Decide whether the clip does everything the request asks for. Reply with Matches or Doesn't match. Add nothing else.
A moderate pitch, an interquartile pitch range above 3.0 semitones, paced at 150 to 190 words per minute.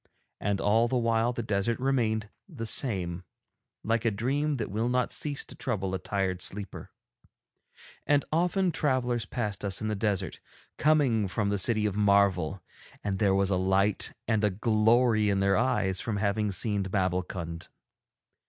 Doesn't match